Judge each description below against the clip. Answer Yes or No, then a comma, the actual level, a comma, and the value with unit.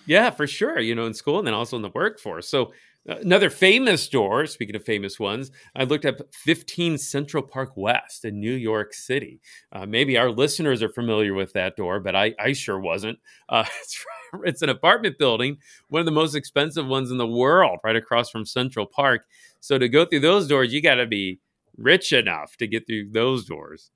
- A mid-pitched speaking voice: No, low, 125 Hz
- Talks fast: Yes, fast, 210 wpm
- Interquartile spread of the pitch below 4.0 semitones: No, average, 5.0 semitones